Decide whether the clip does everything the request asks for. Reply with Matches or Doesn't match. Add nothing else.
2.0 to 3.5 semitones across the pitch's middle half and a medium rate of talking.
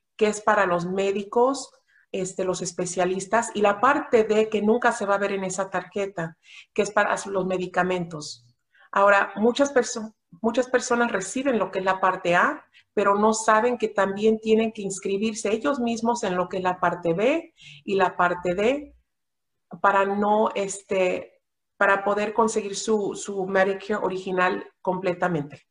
Matches